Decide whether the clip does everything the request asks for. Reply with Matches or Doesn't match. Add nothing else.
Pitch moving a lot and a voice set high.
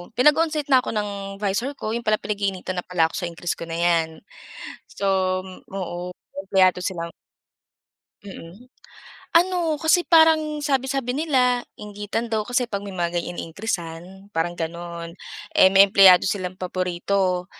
Matches